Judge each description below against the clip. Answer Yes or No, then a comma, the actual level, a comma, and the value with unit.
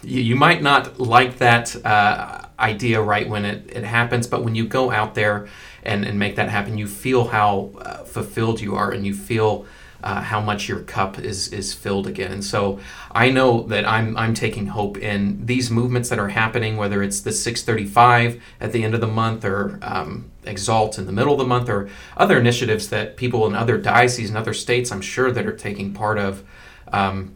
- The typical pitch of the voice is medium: No, low, 110 Hz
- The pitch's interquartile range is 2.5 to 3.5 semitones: Yes, average, 3.0 semitones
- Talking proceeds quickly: Yes, fast, 210 wpm